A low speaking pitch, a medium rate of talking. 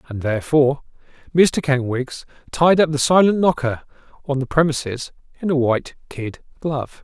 No: medium, 145 Hz; average, 145 wpm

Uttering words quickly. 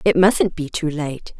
Yes: fast, 215 wpm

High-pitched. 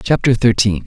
No: low, 105 Hz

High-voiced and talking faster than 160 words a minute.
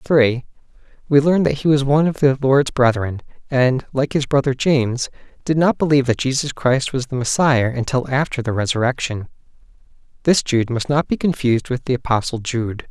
No: low, 130 Hz; average, 180 wpm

